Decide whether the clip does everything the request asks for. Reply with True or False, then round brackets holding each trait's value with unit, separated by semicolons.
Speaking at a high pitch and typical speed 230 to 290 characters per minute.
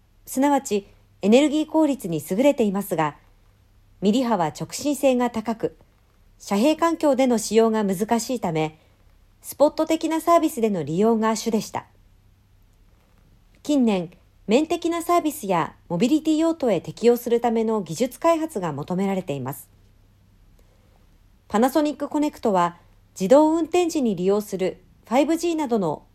True (210 Hz; 285 characters per minute)